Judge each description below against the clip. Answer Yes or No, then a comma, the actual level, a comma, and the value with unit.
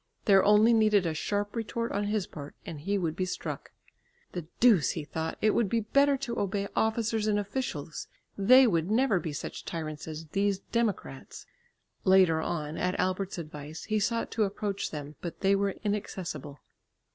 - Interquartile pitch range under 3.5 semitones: No, average, 4.9 semitones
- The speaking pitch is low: No, high, 195 Hz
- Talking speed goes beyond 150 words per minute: Yes, average, 175 wpm